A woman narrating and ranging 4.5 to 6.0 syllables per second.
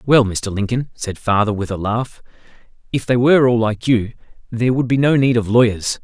No: male; 5.4 syllables/s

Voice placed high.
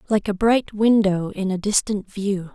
Yes: high, 200 Hz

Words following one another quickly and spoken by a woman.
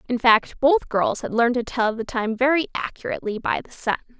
Yes: fast, 215 wpm; female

